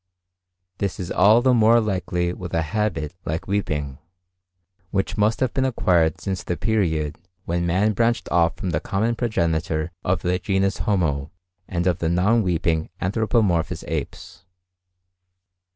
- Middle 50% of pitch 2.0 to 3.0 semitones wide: No, average, 4.3 semitones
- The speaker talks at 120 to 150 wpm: Yes, average, 145 wpm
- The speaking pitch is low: Yes, very low, 90 Hz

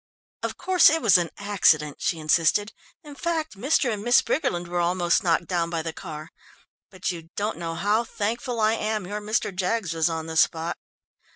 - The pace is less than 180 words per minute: No, average, 190 wpm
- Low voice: No, medium, 185 Hz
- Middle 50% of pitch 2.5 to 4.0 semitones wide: No, average, 4.9 semitones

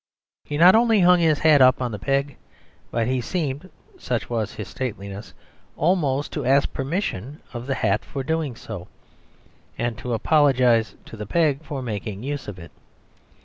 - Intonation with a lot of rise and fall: No, average, 4.8 semitones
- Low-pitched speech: Yes, low, 130 Hz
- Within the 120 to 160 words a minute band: No, average, 170 wpm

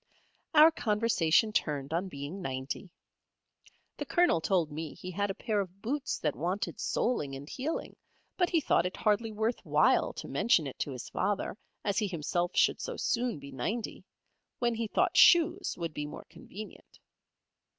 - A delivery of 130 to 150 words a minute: No, average, 170 wpm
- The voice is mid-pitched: No, high, 195 Hz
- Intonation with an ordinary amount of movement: No, wide, 6.7 semitones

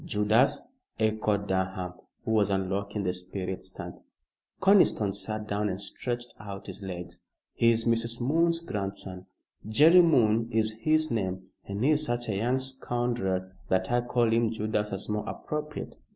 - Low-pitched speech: Yes, low, 110 Hz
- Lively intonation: No, average, 3.7 semitones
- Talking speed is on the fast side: No, average, 150 wpm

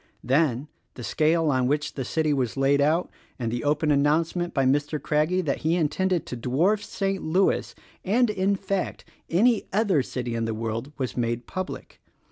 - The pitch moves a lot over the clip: Yes, wide, 5.7 semitones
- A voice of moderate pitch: Yes, medium, 150 Hz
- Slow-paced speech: No, average, 180 wpm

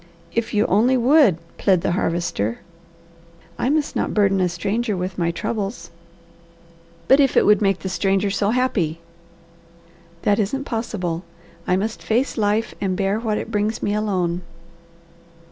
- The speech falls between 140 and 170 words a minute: Yes, average, 150 wpm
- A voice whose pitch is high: Yes, high, 205 Hz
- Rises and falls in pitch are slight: No, average, 3.6 semitones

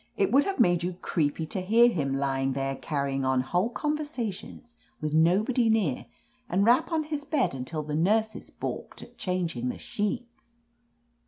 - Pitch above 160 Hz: Yes, medium, 185 Hz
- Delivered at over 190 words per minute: No, average, 165 wpm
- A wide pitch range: Yes, wide, 8.5 semitones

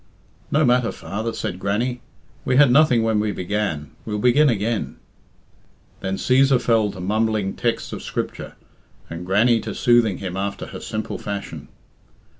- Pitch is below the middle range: Yes, low, 110 Hz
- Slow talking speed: No, average, 150 wpm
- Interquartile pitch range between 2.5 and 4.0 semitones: Yes, average, 3.5 semitones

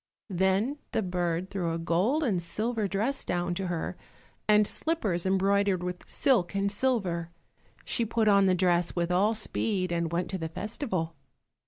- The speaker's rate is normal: Yes, average, 165 wpm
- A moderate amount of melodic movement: Yes, average, 3.4 semitones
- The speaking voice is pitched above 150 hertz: Yes, high, 190 Hz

